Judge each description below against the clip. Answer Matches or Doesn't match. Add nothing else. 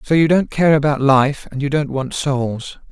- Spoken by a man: Matches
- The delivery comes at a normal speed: Doesn't match